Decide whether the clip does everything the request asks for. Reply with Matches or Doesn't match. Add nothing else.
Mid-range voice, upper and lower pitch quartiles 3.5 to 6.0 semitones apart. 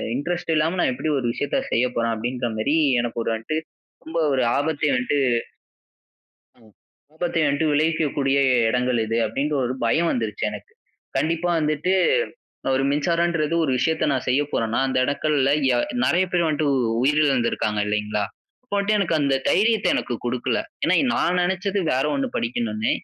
Matches